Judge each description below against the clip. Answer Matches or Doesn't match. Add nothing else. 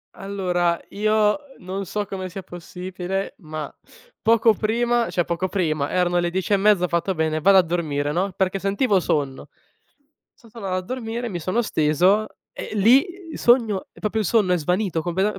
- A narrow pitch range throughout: Doesn't match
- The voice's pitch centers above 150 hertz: Matches